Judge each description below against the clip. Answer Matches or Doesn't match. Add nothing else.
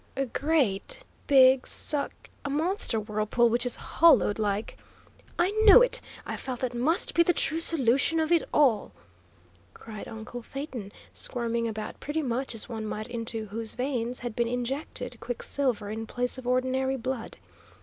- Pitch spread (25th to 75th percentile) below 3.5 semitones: Doesn't match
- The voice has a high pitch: Matches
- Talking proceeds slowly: Doesn't match